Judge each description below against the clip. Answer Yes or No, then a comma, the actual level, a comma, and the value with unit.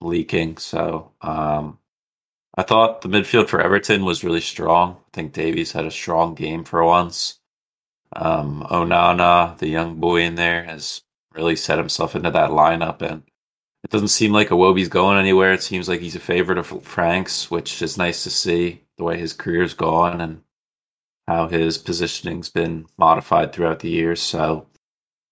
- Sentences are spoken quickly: No, average, 170 wpm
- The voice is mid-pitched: No, very low, 85 Hz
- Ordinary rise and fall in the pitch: No, narrow, 1.4 semitones